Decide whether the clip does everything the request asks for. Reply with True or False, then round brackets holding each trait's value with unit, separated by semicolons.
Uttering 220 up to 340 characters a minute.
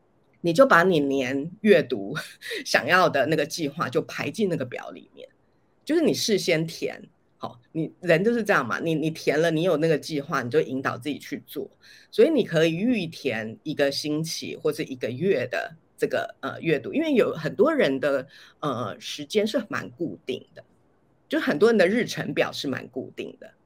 True (265 characters per minute)